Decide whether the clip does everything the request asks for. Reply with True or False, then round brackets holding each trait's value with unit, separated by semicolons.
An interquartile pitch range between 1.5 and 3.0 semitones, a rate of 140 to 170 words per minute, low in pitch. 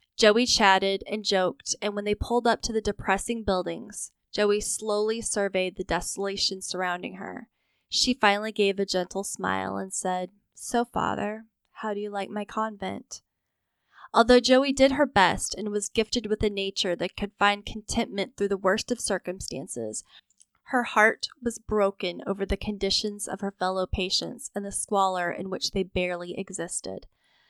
False (2.4 semitones; 165 wpm; 200 Hz)